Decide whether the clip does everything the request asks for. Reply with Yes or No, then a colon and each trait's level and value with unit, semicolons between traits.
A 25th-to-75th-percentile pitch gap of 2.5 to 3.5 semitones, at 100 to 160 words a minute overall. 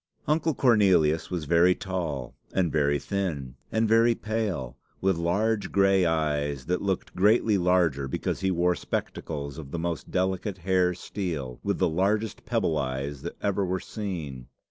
No: average, 4.7 semitones; average, 155 wpm